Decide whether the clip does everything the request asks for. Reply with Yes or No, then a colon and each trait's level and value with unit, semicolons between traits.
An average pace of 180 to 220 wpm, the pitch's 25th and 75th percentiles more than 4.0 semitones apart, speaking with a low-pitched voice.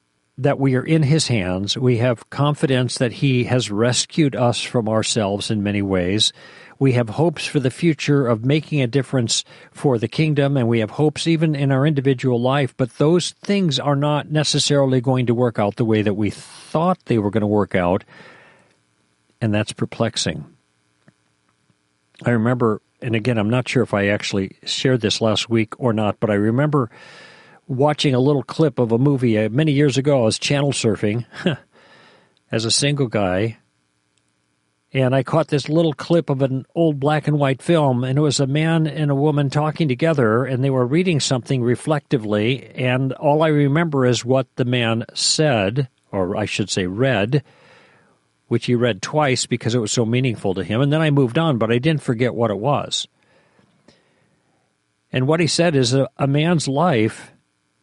Yes: average, 185 wpm; average, 4.9 semitones; low, 130 Hz